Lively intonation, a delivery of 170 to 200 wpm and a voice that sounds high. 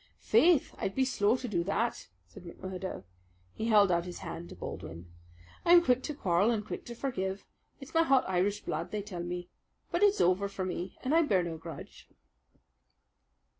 Yes: wide, 6.2 semitones; average, 185 wpm; high, 200 Hz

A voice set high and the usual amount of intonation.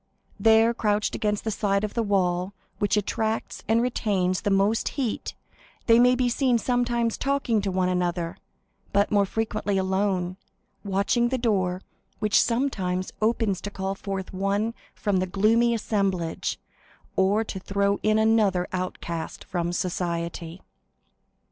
Yes: high, 200 Hz; average, 3.2 semitones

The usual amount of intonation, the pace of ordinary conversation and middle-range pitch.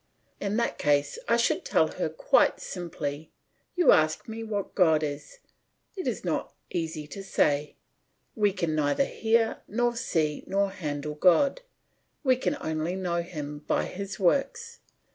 No: wide, 6.5 semitones; average, 150 wpm; medium, 180 Hz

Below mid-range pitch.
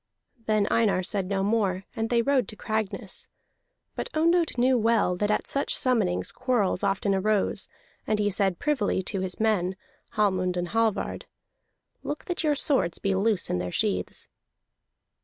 No: high, 210 Hz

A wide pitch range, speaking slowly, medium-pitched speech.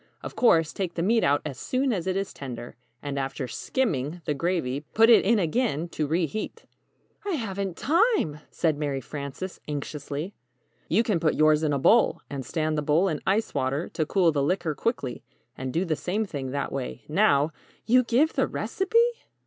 No: wide, 6.4 semitones; average, 195 wpm; medium, 160 Hz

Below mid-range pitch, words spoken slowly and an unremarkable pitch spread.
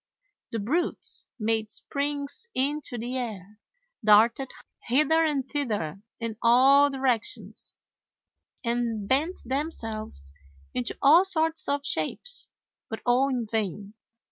No: very high, 250 Hz; slow, 110 wpm; average, 4.6 semitones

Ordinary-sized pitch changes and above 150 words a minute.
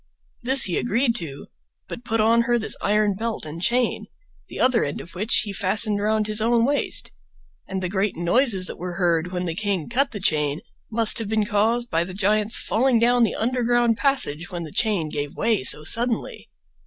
Yes: average, 4.6 semitones; average, 200 wpm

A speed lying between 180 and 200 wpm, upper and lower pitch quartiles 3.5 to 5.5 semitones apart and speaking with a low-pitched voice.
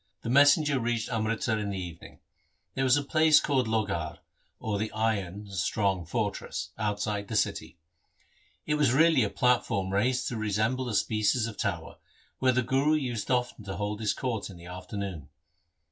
No: average, 170 wpm; average, 4.2 semitones; low, 110 Hz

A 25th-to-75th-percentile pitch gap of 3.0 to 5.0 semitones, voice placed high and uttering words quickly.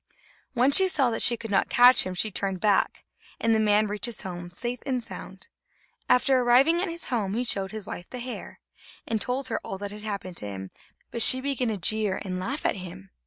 Yes: average, 4.5 semitones; high, 220 Hz; fast, 225 wpm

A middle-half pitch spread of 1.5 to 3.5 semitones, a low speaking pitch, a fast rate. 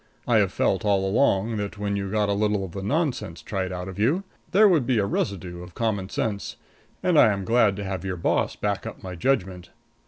Yes: average, 2.8 semitones; low, 100 Hz; fast, 225 wpm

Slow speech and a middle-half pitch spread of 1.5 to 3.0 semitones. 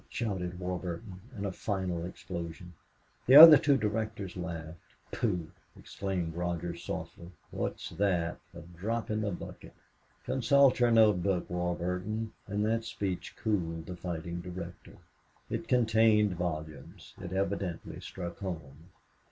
No: slow, 130 wpm; average, 3.7 semitones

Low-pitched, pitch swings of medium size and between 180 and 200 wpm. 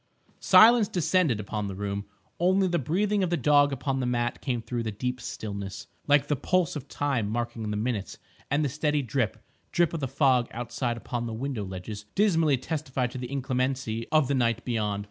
Yes: low, 130 Hz; average, 4.4 semitones; average, 195 wpm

